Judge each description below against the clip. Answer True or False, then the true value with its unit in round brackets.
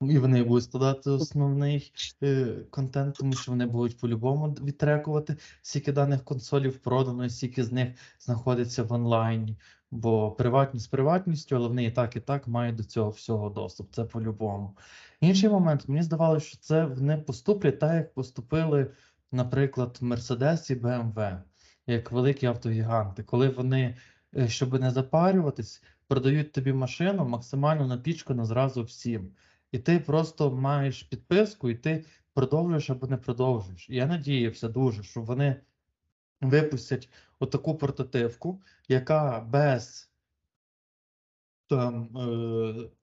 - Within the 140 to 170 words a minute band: False (130 wpm)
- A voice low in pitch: True (130 Hz)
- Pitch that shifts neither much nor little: True (3.3 semitones)